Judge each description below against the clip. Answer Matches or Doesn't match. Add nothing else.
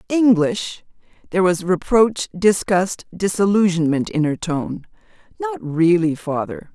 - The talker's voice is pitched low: Doesn't match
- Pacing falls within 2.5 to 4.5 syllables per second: Matches